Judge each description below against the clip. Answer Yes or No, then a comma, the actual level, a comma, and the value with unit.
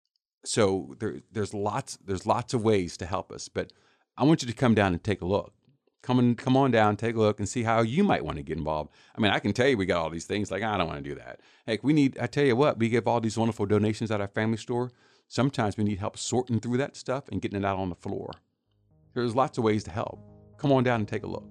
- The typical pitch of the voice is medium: No, low, 110 Hz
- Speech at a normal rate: No, fast, 285 wpm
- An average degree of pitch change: Yes, average, 3.3 semitones